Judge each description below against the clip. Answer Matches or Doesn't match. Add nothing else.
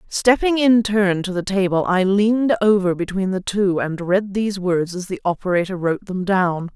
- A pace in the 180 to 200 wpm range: Matches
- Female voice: Matches